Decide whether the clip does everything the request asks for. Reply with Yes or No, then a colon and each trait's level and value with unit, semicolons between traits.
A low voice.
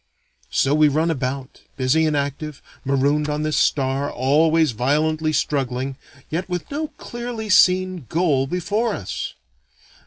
No: medium, 150 Hz